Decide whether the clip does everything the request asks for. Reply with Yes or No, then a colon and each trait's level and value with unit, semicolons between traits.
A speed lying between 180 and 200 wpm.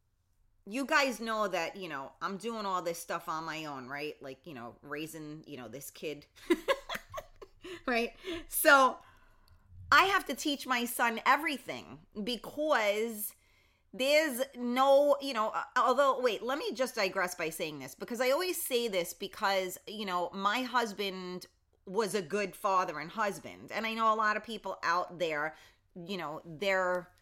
No: average, 165 wpm